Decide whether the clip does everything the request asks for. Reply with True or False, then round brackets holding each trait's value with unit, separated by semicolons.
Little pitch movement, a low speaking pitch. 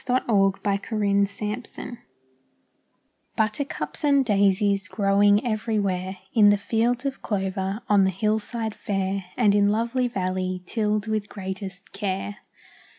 False (2.1 semitones; 205 Hz)